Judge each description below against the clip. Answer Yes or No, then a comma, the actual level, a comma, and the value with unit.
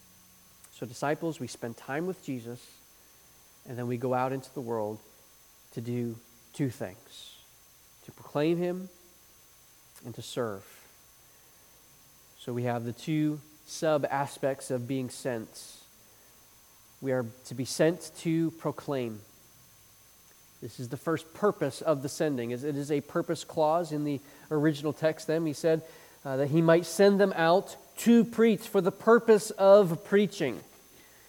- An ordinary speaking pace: Yes, average, 145 wpm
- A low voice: No, medium, 145 Hz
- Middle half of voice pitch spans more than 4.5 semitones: Yes, average, 5.0 semitones